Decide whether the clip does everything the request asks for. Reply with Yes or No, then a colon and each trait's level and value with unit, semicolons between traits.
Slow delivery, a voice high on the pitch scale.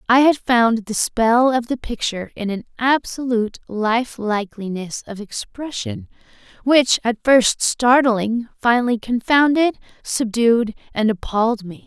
Yes: slow, 125 wpm; high, 235 Hz